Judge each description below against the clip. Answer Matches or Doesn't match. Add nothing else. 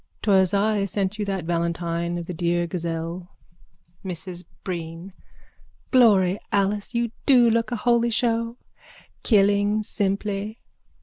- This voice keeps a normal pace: Doesn't match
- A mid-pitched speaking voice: Doesn't match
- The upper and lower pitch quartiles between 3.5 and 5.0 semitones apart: Matches